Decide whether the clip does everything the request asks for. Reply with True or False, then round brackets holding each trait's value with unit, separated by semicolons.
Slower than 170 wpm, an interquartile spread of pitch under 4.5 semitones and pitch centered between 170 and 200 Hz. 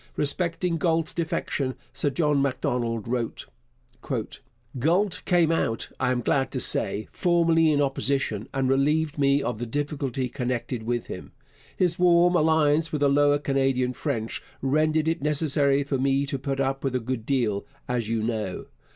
False (160 wpm; 3.8 semitones; 140 Hz)